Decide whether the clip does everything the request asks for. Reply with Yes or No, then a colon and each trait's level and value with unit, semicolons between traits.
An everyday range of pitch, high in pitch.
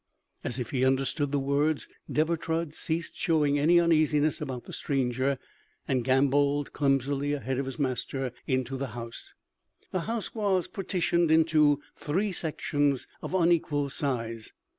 No: average, 3.4 semitones; medium, 145 Hz